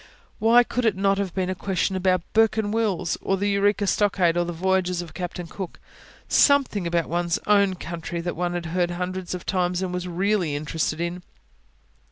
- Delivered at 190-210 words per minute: Yes, average, 195 wpm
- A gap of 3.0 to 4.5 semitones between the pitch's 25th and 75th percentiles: No, narrow, 2.4 semitones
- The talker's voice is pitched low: No, medium, 185 Hz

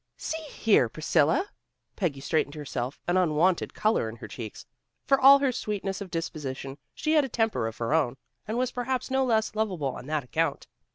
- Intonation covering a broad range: Yes, wide, 8.9 semitones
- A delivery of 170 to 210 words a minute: Yes, average, 185 wpm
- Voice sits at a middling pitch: Yes, medium, 180 Hz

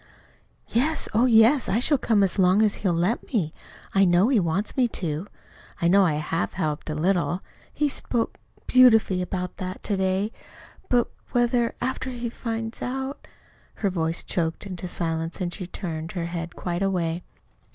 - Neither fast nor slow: Yes, average, 170 wpm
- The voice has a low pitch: No, high, 190 Hz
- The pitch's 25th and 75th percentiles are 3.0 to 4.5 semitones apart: No, average, 5.1 semitones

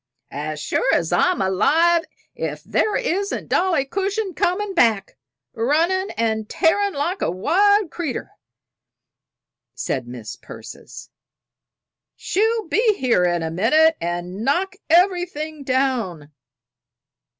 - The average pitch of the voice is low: No, very high, 300 Hz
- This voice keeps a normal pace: No, slow, 115 wpm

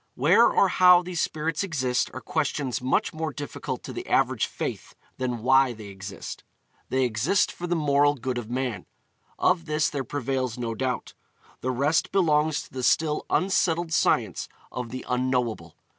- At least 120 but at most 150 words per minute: No, average, 165 wpm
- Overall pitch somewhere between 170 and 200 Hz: No, low, 135 Hz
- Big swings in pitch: No, average, 4.1 semitones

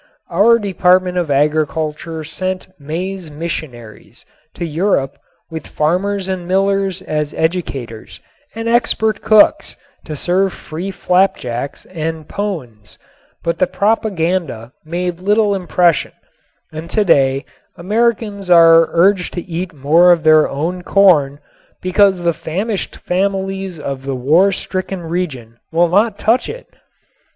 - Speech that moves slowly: Yes, slow, 120 wpm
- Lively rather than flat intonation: No, average, 3.8 semitones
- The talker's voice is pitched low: No, medium, 175 Hz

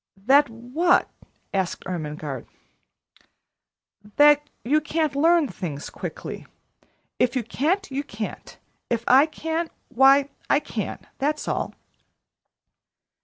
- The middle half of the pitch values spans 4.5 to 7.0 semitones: Yes, average, 5.0 semitones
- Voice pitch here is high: Yes, very high, 275 Hz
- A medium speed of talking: No, slow, 105 wpm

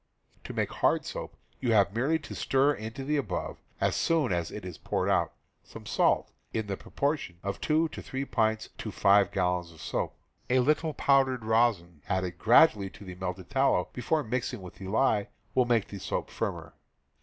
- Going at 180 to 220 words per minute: Yes, average, 190 wpm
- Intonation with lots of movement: Yes, wide, 5.8 semitones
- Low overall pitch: Yes, low, 110 Hz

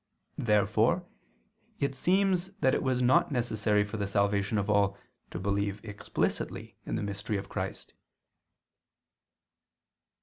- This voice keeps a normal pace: No, slow, 125 wpm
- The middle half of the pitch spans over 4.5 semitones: No, average, 4.2 semitones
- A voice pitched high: No, low, 105 Hz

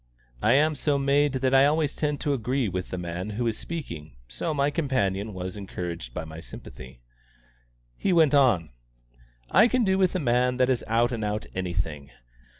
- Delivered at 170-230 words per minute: Yes, average, 185 wpm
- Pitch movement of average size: No, wide, 7.8 semitones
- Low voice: Yes, low, 120 Hz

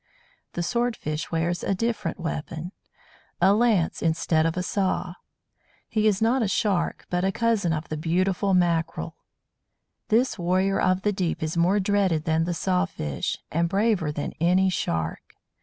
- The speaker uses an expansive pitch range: No, average, 3.4 semitones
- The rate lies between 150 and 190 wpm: Yes, average, 160 wpm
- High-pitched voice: No, medium, 180 Hz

